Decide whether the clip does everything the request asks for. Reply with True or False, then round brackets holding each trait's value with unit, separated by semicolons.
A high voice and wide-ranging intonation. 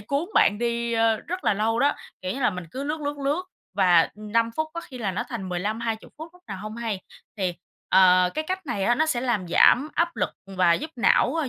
True (230 Hz; 6.7 semitones)